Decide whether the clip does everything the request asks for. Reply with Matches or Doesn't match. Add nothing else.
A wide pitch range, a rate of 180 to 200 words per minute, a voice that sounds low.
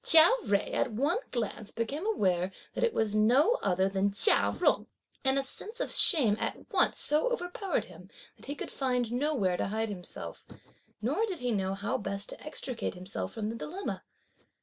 Doesn't match